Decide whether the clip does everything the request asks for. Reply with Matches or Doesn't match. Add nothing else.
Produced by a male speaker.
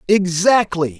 Matches